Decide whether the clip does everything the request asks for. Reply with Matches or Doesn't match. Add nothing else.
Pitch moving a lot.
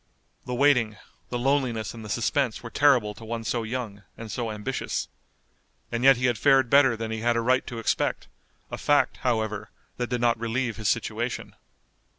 Doesn't match